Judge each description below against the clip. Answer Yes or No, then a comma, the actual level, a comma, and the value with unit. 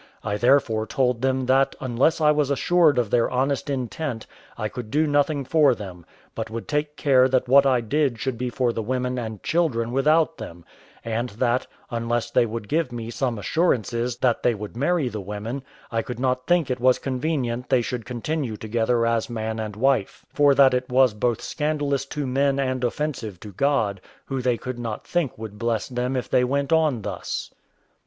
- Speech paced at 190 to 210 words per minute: Yes, average, 195 wpm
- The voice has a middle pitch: No, low, 125 Hz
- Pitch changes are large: No, average, 3.3 semitones